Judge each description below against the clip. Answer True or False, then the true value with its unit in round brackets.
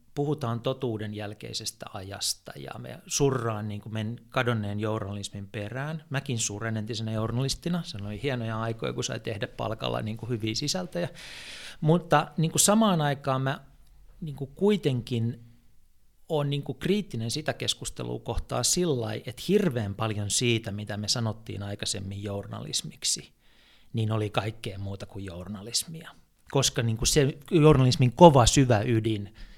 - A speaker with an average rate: True (140 wpm)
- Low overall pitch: True (120 Hz)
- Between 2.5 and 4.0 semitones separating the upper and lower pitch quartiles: False (5.0 semitones)